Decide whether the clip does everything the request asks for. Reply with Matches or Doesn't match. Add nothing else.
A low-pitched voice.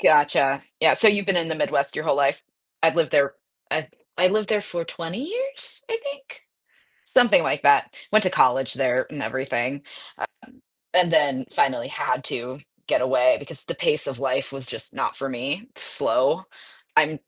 Doesn't match